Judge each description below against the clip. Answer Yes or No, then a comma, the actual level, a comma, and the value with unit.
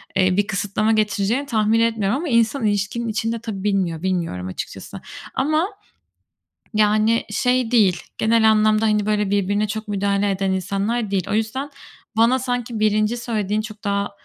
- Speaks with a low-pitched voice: No, high, 215 Hz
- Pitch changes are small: Yes, narrow, 2.3 semitones